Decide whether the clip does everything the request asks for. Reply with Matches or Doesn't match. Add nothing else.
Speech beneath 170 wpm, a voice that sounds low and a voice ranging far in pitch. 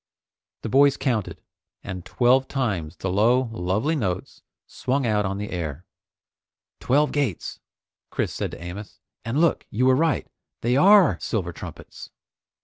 Matches